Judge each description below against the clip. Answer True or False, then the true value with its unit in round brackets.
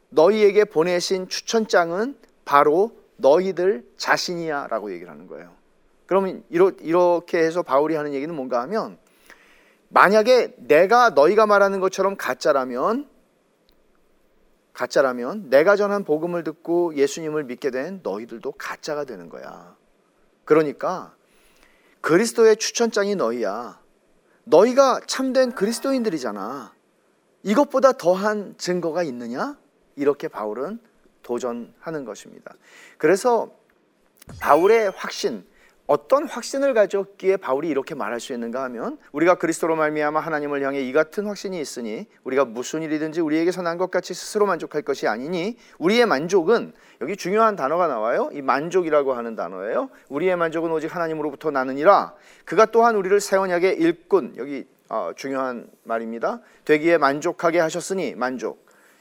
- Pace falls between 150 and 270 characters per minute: False (335 characters per minute)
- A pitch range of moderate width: False (6.1 semitones)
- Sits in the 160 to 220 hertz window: True (185 Hz)